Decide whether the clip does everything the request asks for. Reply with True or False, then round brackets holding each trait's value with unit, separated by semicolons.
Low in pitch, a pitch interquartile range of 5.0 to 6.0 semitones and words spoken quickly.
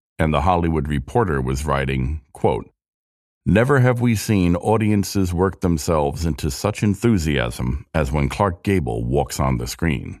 False (80 Hz; 5.5 semitones; 145 wpm)